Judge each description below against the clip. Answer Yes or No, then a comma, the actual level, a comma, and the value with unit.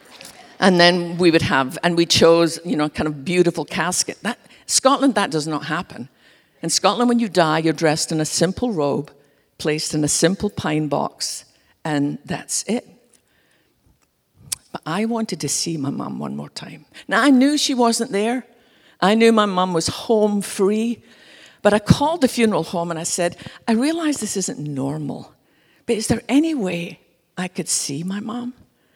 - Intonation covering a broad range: Yes, wide, 6.4 semitones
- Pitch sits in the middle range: Yes, medium, 180 Hz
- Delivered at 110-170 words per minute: No, average, 180 wpm